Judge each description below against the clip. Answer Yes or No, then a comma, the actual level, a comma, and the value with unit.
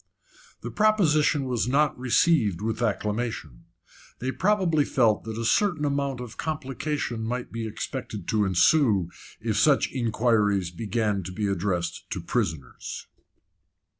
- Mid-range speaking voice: No, low, 115 Hz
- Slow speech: Yes, slow, 130 wpm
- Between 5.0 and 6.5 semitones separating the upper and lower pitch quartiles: Yes, average, 5.3 semitones